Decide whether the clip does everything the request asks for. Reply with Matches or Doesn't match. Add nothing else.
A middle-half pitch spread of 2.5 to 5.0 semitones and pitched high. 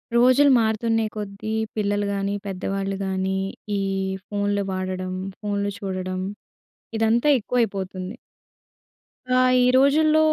Matches